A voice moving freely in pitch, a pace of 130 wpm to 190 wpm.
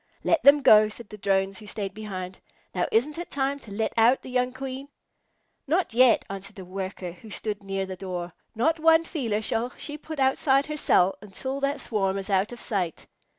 No: wide, 5.8 semitones; average, 200 wpm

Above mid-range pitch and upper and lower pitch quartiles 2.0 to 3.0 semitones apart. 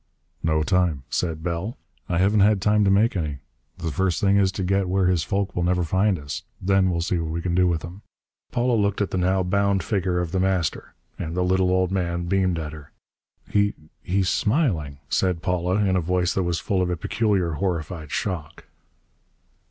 No: very low, 90 Hz; narrow, 2.4 semitones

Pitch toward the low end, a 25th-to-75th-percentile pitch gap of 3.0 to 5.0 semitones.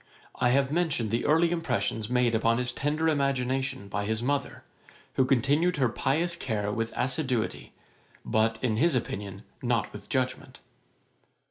Yes: low, 125 Hz; average, 4.2 semitones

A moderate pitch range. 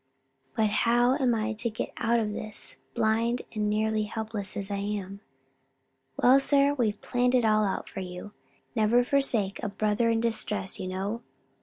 No: narrow, 2.3 semitones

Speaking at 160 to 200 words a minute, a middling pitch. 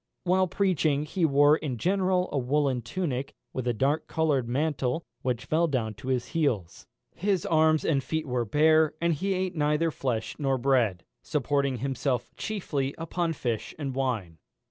Yes: average, 165 wpm; medium, 145 Hz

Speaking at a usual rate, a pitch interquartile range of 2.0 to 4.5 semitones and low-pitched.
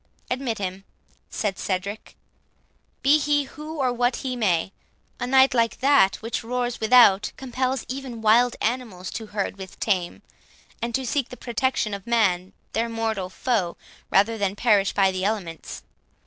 No: average, 150 wpm; average, 4.2 semitones; high, 230 Hz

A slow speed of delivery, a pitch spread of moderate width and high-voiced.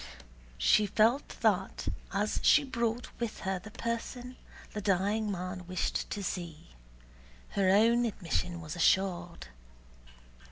Yes: slow, 120 wpm; average, 4.2 semitones; high, 200 Hz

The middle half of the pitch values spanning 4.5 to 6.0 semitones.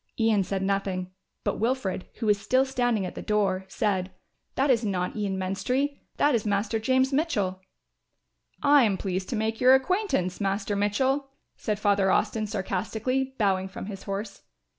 Yes: average, 4.8 semitones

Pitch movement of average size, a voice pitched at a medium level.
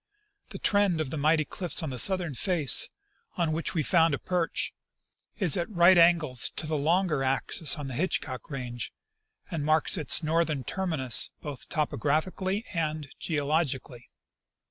Yes: average, 3.4 semitones; medium, 155 Hz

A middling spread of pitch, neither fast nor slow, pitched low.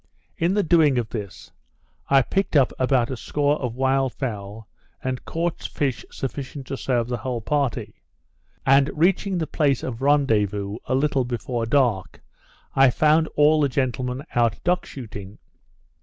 Yes: average, 3.8 semitones; average, 155 wpm; low, 130 Hz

